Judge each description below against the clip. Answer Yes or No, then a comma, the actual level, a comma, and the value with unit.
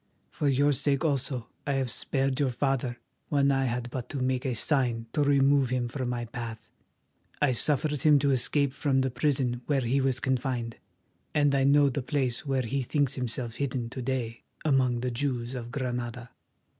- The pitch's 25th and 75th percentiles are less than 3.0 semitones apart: Yes, narrow, 2.4 semitones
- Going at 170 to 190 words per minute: Yes, average, 185 wpm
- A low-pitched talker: Yes, low, 130 Hz